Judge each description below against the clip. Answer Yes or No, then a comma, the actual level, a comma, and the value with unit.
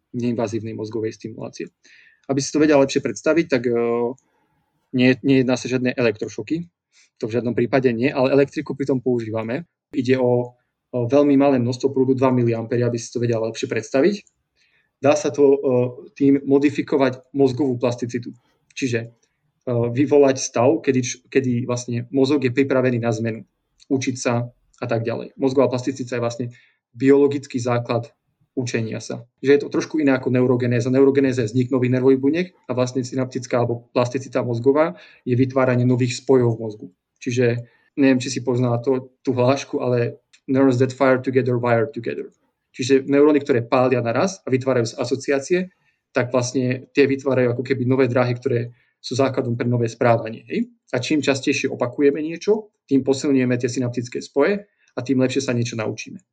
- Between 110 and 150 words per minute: No, average, 160 wpm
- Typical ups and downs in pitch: No, narrow, 2.1 semitones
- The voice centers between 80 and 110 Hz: No, low, 130 Hz